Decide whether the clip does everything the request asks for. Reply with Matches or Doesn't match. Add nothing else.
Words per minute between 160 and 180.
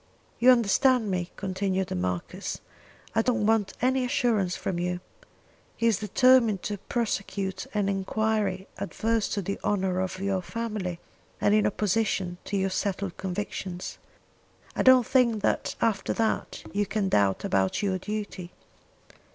Doesn't match